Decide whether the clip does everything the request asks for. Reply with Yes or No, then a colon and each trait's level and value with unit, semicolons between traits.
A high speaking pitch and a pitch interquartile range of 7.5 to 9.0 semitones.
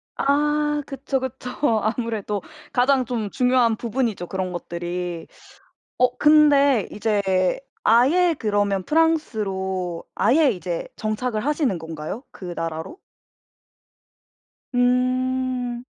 No: high, 240 Hz; wide, 5.6 semitones